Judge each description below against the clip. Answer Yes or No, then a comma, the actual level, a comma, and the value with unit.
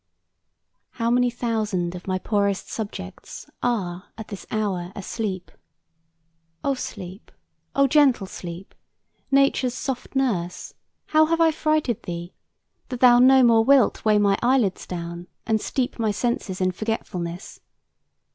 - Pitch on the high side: Yes, high, 220 Hz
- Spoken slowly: Yes, slow, 130 wpm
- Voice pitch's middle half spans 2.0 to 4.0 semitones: No, average, 5.1 semitones